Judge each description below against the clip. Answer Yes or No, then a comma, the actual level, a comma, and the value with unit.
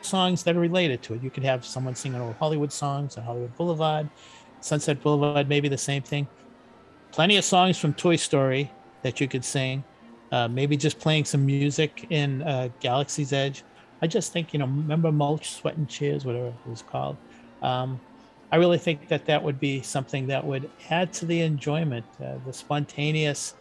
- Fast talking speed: No, average, 190 wpm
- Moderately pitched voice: Yes, medium, 145 Hz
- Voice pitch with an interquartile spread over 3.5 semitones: No, average, 3.0 semitones